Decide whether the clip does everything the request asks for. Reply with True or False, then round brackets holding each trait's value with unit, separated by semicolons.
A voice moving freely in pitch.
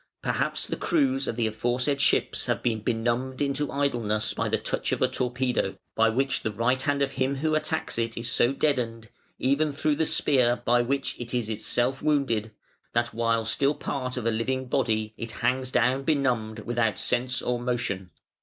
False (3.0 semitones)